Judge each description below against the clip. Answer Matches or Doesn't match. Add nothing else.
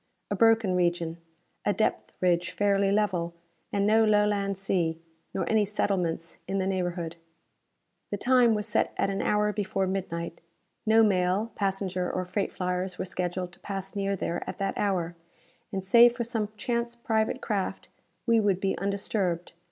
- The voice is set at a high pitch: Matches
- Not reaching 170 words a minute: Matches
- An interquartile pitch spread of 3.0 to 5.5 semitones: Doesn't match